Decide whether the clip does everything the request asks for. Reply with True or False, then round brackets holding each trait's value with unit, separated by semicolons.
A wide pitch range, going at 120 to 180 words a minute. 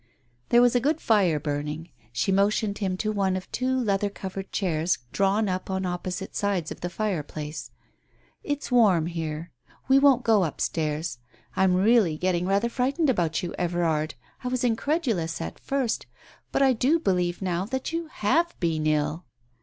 True (5.8 semitones; 170 wpm)